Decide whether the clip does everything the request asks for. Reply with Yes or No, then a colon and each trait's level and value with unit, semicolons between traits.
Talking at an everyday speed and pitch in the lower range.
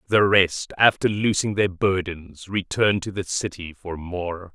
Yes: average, 160 wpm; very low, 95 Hz